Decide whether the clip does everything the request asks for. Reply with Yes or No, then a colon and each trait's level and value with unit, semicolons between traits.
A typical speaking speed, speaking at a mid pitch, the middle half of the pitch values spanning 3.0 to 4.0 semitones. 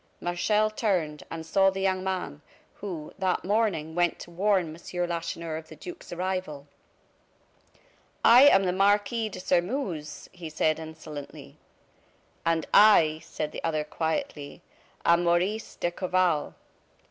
No: slow, 130 wpm; medium, 175 Hz; average, 3.4 semitones